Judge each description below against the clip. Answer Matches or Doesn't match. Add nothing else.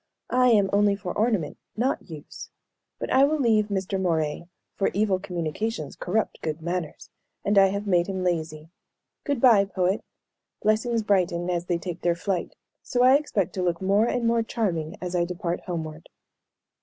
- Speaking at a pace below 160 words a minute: Doesn't match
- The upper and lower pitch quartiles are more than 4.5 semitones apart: Doesn't match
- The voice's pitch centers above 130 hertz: Matches